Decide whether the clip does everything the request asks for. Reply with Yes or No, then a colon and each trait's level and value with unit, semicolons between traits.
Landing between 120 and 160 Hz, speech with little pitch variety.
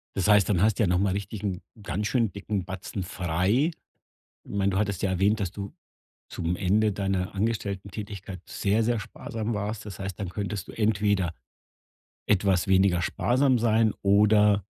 No: low, 100 Hz; narrow, 2.0 semitones